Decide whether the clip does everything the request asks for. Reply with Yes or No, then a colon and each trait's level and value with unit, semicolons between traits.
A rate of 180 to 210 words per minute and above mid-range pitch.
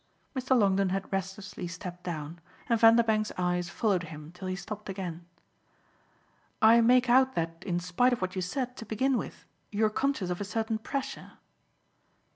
No: average, 165 wpm; high, 200 Hz